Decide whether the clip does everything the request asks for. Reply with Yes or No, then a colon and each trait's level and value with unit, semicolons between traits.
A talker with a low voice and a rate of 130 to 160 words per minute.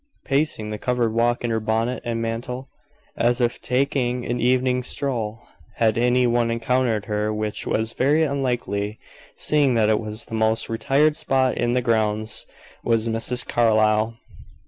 Yes: low, 120 Hz; average, 155 wpm